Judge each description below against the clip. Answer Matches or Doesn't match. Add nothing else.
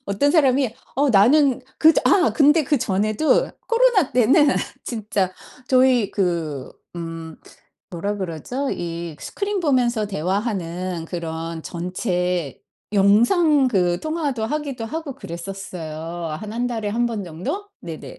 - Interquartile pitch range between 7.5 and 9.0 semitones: Matches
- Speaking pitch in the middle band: Doesn't match